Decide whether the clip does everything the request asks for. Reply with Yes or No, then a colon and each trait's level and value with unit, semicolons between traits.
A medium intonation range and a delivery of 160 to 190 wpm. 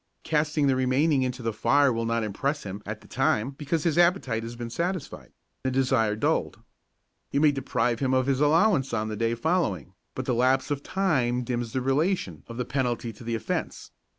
No: average, 4.0 semitones; fast, 205 wpm